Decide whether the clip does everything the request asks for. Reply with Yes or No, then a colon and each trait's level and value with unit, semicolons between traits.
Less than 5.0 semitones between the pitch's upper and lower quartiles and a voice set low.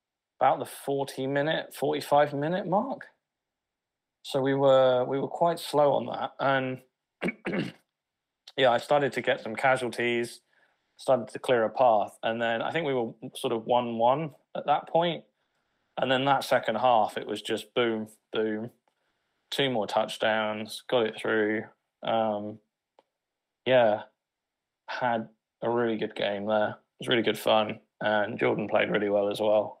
Yes: average, 3.9 semitones; low, 120 Hz